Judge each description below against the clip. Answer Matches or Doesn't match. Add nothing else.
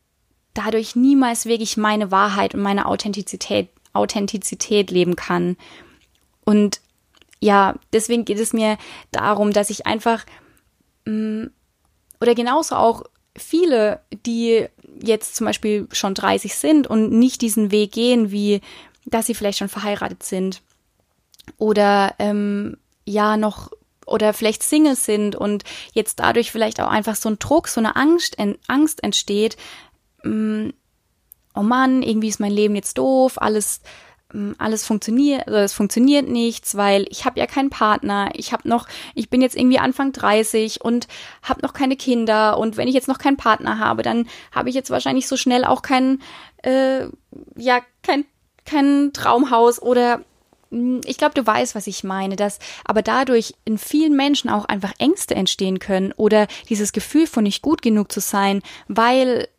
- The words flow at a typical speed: Matches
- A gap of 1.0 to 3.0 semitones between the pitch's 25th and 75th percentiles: Doesn't match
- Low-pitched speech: Doesn't match